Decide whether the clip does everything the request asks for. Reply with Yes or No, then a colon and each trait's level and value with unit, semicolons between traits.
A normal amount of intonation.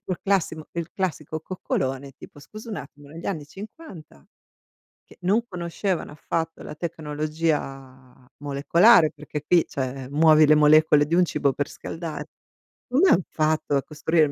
Yes: average, 3.1 semitones